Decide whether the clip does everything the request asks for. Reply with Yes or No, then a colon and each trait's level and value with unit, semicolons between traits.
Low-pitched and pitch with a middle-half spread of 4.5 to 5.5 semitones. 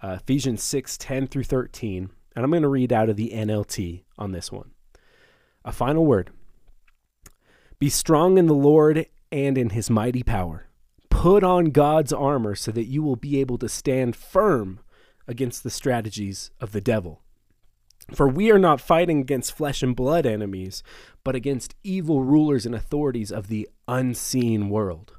Yes: low, 125 Hz; average, 5.0 semitones